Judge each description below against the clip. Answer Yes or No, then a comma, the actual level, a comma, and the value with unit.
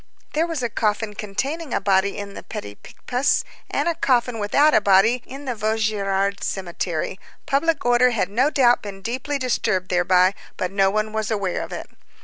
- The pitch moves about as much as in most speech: Yes, average, 4.4 semitones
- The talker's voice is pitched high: Yes, high, 215 Hz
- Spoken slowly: No, average, 180 wpm